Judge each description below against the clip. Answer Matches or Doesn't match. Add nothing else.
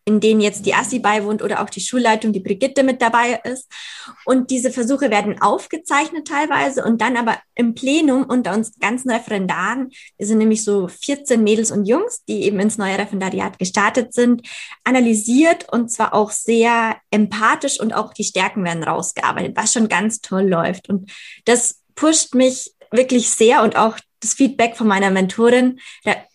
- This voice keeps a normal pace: Matches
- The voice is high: Matches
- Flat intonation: Doesn't match